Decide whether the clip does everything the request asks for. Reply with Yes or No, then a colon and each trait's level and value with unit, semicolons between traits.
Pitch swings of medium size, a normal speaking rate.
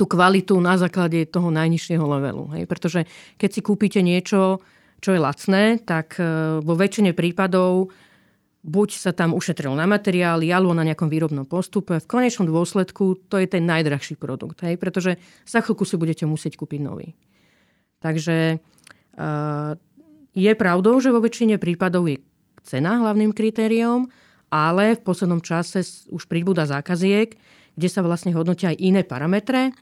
Yes: average, 3.4 semitones; average, 145 wpm